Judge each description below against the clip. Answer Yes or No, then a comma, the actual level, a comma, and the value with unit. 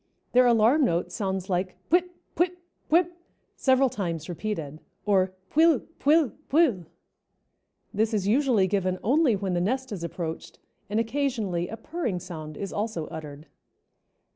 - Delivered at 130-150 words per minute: Yes, average, 140 wpm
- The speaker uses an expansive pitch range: Yes, wide, 6.7 semitones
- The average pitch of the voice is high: Yes, high, 210 Hz